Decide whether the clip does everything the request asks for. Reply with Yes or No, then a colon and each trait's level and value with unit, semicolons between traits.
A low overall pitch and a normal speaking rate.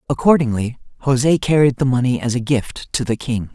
Yes: low, 130 Hz; average, 185 wpm